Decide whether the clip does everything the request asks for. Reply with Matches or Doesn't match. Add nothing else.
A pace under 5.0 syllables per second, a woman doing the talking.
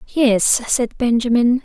Matches